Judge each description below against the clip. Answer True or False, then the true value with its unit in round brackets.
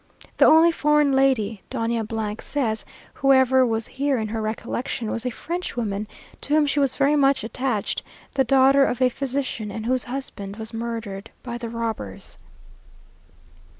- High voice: True (245 Hz)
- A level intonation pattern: False (3.6 semitones)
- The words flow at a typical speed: True (150 wpm)